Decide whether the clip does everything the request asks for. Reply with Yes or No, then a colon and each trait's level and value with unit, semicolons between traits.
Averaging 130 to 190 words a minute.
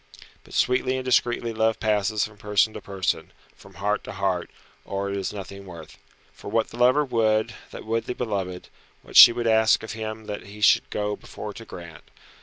No: average, 200 wpm